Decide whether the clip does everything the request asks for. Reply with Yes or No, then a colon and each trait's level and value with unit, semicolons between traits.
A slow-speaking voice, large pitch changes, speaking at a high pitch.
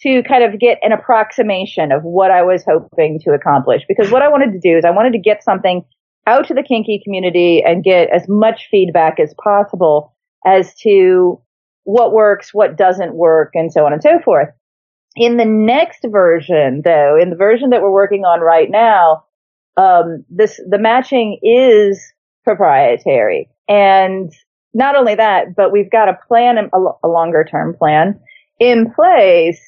No: average, 175 wpm; wide, 5.8 semitones; high, 205 Hz